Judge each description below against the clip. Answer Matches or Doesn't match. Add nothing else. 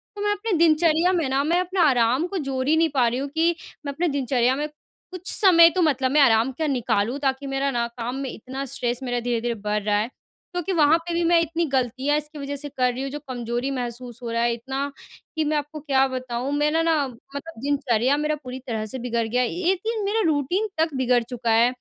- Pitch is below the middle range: Doesn't match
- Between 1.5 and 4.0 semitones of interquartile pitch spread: Doesn't match